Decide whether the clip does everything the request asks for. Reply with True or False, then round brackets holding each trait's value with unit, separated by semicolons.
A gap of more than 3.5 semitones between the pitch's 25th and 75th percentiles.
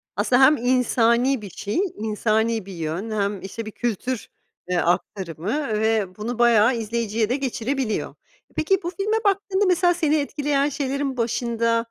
True (4.5 semitones)